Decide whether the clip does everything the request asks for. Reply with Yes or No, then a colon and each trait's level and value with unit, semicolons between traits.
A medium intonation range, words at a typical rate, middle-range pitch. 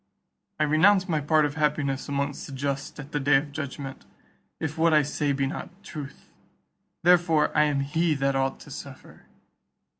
No: narrow, 2.2 semitones; average, 175 wpm; medium, 145 Hz